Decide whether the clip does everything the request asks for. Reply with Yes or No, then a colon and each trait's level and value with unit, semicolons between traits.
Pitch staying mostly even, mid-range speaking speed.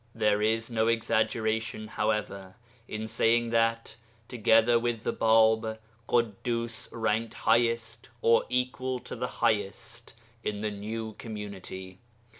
No: narrow, 1.4 semitones; slow, 115 wpm